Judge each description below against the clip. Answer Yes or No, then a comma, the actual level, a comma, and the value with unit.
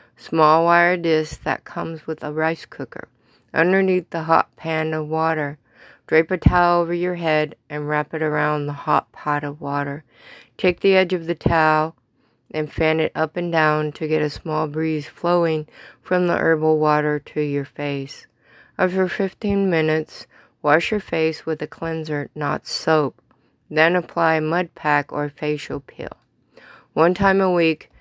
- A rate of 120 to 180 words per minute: Yes, average, 165 wpm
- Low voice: No, medium, 160 Hz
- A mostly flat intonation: Yes, narrow, 2.2 semitones